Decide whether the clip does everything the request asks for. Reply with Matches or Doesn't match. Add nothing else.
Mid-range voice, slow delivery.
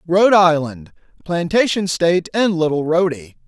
Matches